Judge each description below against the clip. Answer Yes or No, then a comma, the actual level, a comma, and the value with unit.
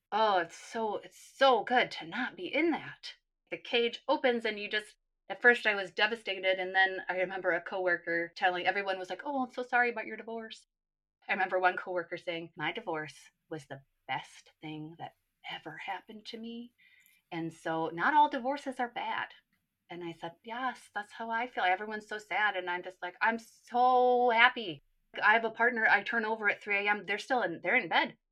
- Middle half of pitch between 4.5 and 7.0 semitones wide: Yes, average, 4.9 semitones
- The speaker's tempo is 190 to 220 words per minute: Yes, fast, 205 wpm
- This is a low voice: No, high, 210 Hz